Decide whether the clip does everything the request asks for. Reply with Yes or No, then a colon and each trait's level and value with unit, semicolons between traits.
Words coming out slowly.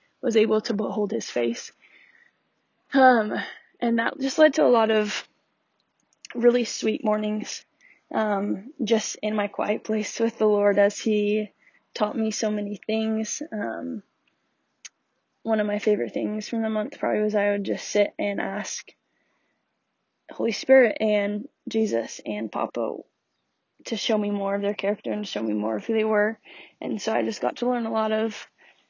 No: average, 170 wpm